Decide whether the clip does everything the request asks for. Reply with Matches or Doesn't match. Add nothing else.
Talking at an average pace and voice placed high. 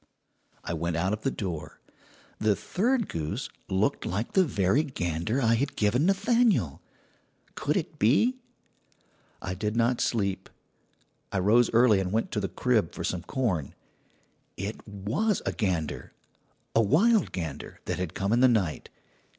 Doesn't match